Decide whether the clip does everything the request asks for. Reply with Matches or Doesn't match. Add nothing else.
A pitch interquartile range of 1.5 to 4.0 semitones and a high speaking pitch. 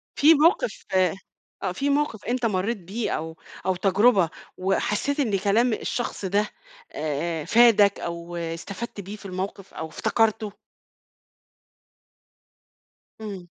Doesn't match